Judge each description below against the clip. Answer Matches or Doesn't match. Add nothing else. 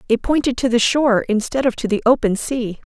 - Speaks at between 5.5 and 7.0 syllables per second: Matches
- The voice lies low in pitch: Doesn't match